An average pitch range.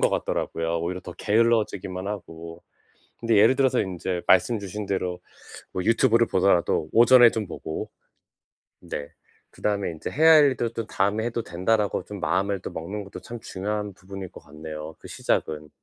Yes: average, 4.3 semitones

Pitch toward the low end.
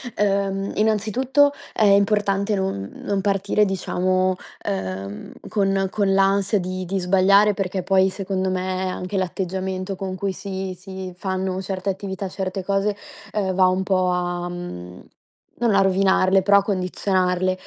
No: high, 190 Hz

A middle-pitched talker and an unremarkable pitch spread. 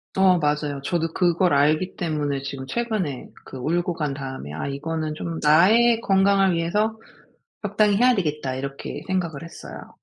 Yes: medium, 165 Hz; average, 5.0 semitones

